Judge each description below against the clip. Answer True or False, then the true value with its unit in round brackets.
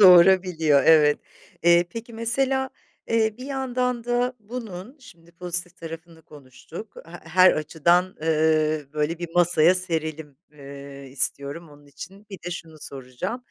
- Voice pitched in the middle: True (170 Hz)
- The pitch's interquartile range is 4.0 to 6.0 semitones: True (5.2 semitones)